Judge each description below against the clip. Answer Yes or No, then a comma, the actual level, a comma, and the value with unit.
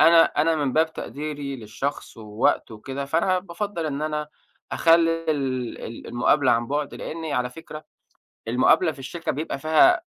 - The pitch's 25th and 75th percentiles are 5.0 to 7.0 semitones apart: No, average, 3.7 semitones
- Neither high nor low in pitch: Yes, medium, 150 Hz